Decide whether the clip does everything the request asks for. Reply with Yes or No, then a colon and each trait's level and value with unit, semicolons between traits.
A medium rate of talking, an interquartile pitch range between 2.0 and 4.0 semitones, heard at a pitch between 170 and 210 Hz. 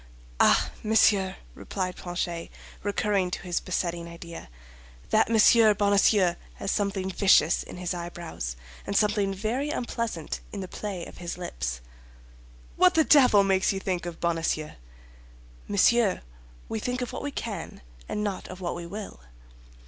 Yes: average, 150 wpm; average, 3.3 semitones; high, 190 Hz